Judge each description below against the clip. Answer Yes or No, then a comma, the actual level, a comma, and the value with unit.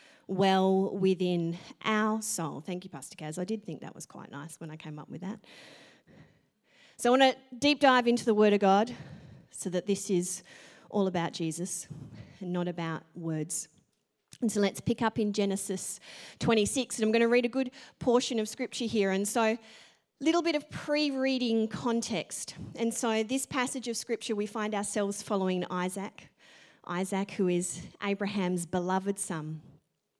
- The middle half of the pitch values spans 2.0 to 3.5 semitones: No, average, 4.4 semitones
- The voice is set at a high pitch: Yes, high, 200 Hz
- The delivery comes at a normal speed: Yes, average, 175 wpm